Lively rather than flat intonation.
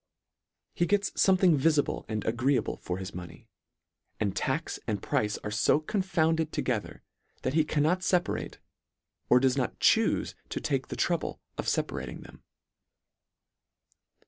Yes: wide, 6.9 semitones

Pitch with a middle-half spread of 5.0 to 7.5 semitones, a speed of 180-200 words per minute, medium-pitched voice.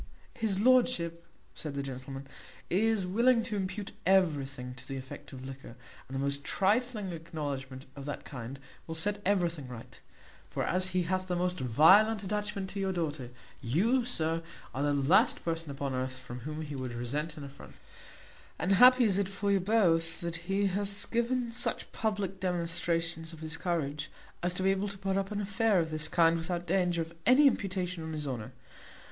Yes: wide, 5.5 semitones; average, 185 wpm; medium, 170 Hz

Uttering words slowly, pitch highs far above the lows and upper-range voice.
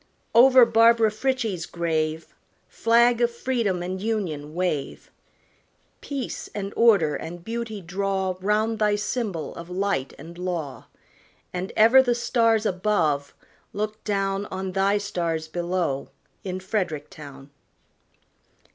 No: slow, 120 wpm; average, 4.7 semitones; high, 195 Hz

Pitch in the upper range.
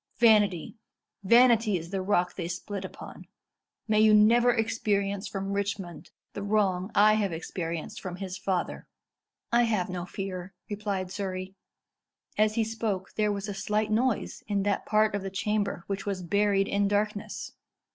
Yes: high, 200 Hz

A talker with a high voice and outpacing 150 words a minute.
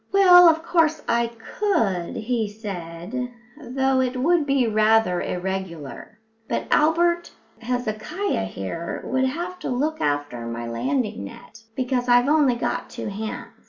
No: high, 245 Hz; slow, 135 wpm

